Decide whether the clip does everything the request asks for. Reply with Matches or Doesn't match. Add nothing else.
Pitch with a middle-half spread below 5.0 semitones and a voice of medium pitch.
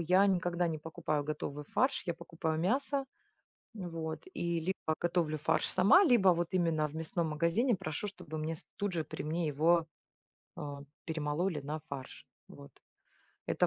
Matches